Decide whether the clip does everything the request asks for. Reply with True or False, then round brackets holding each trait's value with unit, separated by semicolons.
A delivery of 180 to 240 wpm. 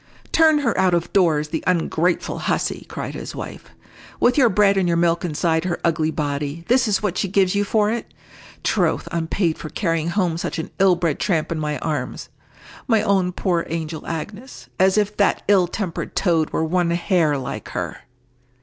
True (190 wpm)